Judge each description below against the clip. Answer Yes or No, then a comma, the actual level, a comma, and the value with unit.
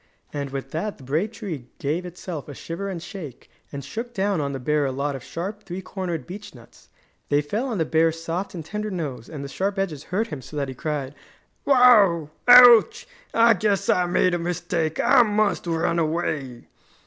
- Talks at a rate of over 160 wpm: Yes, average, 200 wpm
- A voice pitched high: No, medium, 170 Hz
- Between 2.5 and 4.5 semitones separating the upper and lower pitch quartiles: No, wide, 5.6 semitones